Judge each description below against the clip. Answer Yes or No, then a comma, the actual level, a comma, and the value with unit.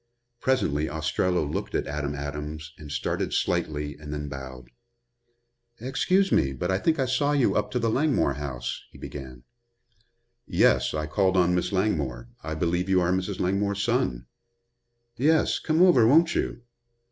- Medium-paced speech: Yes, average, 160 wpm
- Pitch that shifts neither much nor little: No, wide, 7.5 semitones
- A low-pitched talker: Yes, very low, 85 Hz